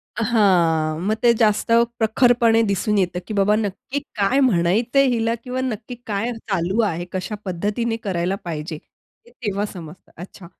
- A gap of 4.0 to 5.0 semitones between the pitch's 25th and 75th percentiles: Yes, average, 4.5 semitones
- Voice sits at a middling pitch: No, high, 205 Hz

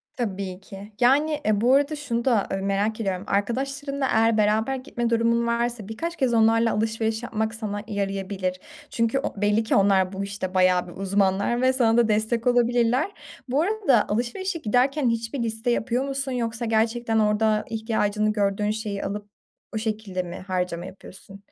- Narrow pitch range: No, average, 3.1 semitones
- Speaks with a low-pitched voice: No, high, 220 Hz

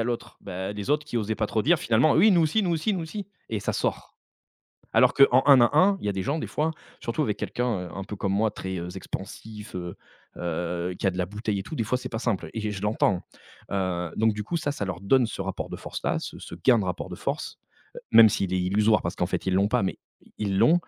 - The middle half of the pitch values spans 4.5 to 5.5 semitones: Yes, average, 5.1 semitones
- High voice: No, low, 105 Hz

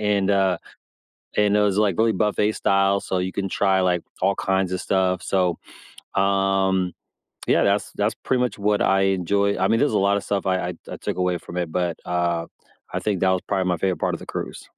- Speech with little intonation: Yes, narrow, 1.7 semitones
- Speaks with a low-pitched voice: Yes, very low, 95 Hz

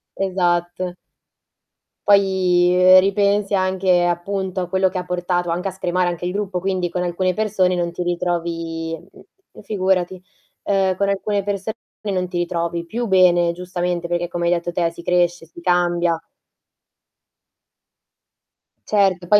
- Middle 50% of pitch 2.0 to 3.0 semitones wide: No, narrow, 1.6 semitones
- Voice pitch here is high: No, medium, 180 Hz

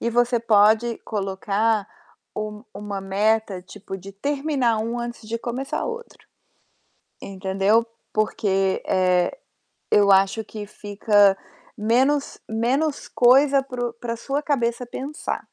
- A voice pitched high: Yes, high, 220 Hz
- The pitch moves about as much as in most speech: Yes, average, 3.3 semitones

